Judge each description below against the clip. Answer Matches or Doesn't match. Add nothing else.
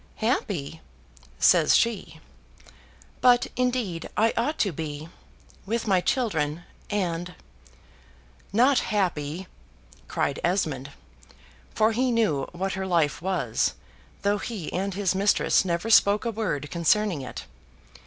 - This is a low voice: Doesn't match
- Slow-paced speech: Matches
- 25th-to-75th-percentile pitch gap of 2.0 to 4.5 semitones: Doesn't match